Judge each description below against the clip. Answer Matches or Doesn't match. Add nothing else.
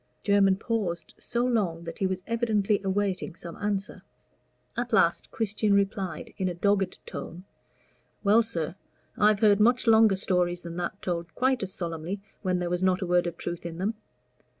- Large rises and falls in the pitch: Doesn't match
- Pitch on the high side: Matches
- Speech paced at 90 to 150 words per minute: Doesn't match